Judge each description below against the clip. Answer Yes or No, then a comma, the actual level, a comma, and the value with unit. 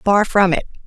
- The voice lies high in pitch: Yes, high, 195 Hz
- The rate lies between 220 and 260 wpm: No, fast, 210 wpm